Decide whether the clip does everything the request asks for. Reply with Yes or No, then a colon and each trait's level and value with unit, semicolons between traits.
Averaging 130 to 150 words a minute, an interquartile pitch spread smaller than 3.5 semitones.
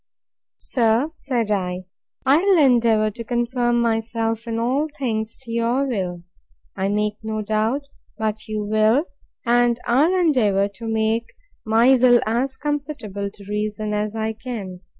Yes: average, 145 wpm; average, 2.7 semitones